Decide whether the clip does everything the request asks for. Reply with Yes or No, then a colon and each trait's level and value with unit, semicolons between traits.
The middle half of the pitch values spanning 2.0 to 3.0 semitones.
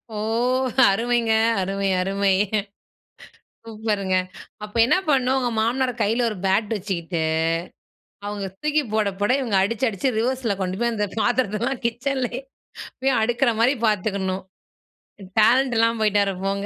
No: average, 3.8 semitones